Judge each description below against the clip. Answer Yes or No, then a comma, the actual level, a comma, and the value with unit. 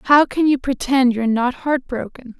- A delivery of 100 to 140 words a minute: No, average, 200 wpm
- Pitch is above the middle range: Yes, very high, 260 Hz